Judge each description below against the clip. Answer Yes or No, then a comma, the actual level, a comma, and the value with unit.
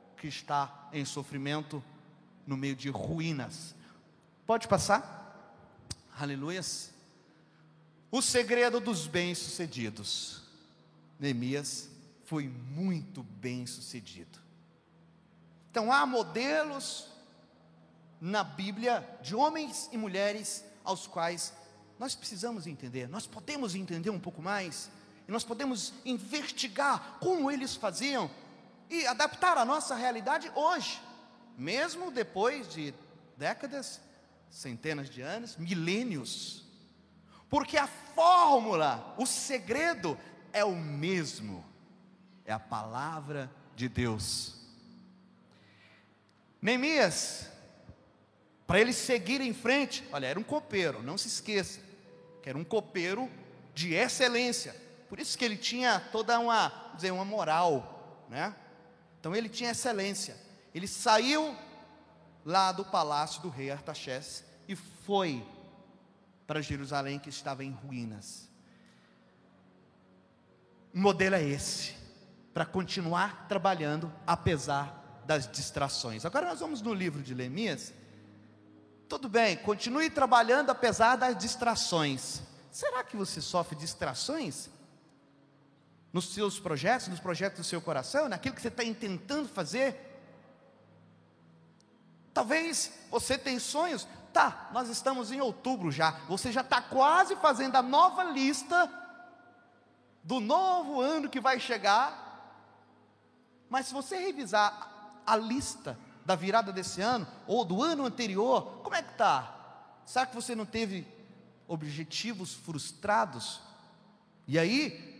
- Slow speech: Yes, slow, 115 wpm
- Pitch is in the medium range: No, high, 195 Hz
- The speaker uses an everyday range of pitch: No, wide, 8.5 semitones